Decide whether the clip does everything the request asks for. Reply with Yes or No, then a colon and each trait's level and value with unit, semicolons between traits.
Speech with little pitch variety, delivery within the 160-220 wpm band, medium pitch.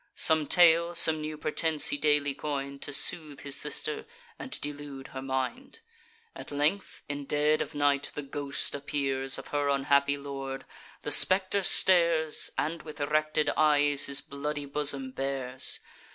No: narrow, 1.9 semitones; average, 150 wpm; medium, 145 Hz